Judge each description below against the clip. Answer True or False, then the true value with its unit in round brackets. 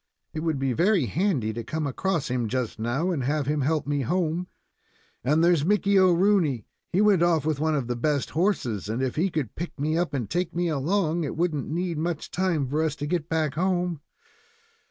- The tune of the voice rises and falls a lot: False (4.3 semitones)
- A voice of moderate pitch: True (155 Hz)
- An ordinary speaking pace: False (210 wpm)